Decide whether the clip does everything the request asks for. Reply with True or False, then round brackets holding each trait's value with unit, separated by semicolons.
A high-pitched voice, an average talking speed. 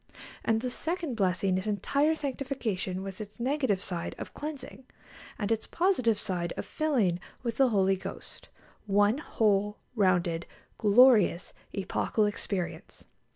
False (210 Hz; 130 wpm)